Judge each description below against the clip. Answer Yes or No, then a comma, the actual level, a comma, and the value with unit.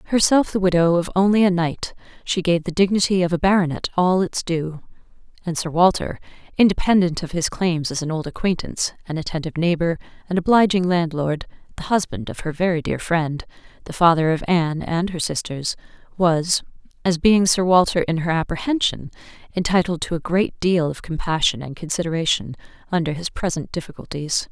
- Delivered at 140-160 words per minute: No, average, 170 wpm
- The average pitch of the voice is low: No, medium, 170 Hz